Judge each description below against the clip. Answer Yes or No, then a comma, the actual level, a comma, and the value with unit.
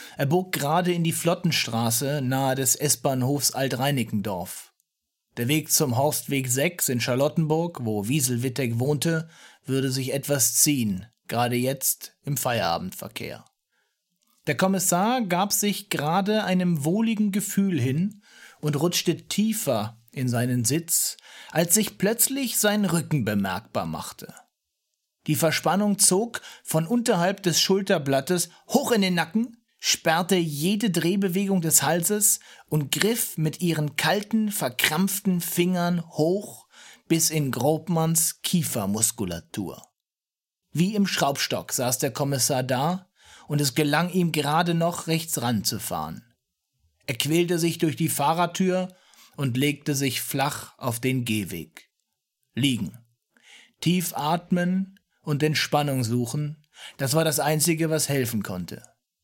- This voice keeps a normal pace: No, slow, 120 wpm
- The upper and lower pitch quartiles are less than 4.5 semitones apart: No, average, 5.2 semitones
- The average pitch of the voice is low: No, medium, 155 Hz